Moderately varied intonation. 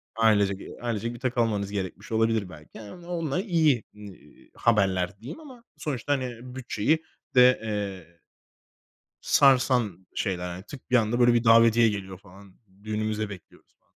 Yes: average, 4.1 semitones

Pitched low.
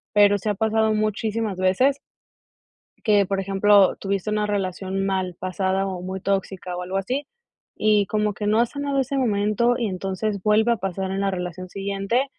No: high, 200 Hz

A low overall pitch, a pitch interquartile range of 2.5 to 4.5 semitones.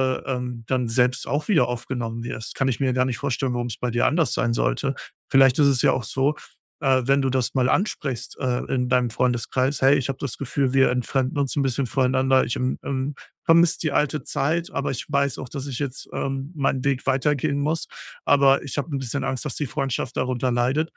No: low, 130 Hz; narrow, 2.0 semitones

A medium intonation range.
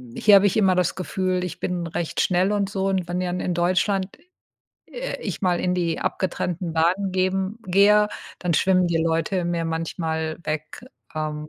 No: narrow, 2.3 semitones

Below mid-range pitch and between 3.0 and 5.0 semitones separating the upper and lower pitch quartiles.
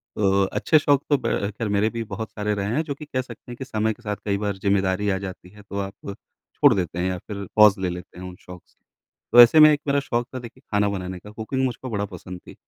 Yes: low, 105 Hz; average, 3.9 semitones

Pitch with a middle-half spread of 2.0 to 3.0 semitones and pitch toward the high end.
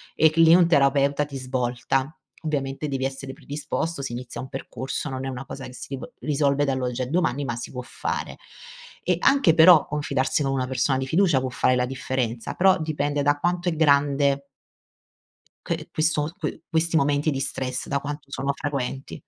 No: narrow, 2.5 semitones; medium, 140 Hz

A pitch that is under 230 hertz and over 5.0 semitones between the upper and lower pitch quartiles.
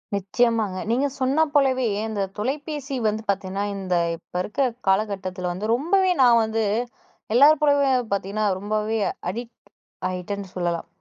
Yes: high, 220 Hz; wide, 5.4 semitones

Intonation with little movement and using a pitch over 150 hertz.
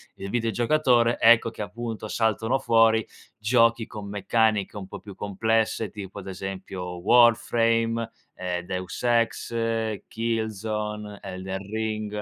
No: narrow, 2.3 semitones; low, 110 Hz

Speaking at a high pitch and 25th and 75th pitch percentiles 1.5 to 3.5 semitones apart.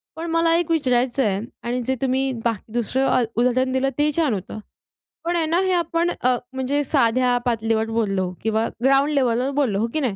No: very high, 255 Hz; average, 4.2 semitones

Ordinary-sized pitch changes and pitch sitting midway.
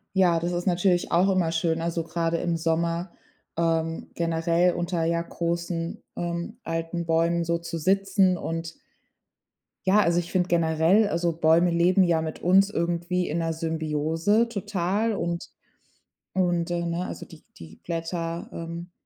No: narrow, 1.3 semitones; medium, 170 Hz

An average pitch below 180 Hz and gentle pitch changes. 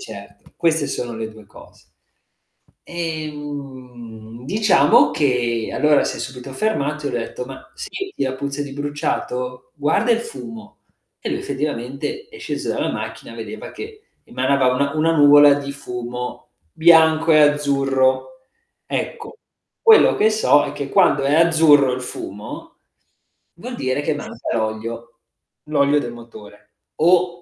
No: medium, 140 Hz; average, 4.1 semitones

